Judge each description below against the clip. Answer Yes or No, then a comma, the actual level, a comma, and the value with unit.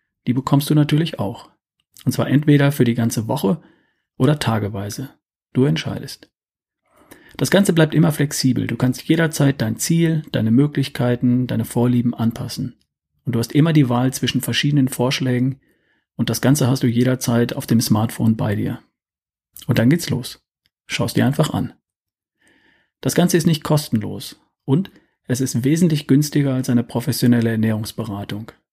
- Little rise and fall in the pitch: No, average, 3.5 semitones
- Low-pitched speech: Yes, low, 130 Hz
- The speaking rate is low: No, average, 155 wpm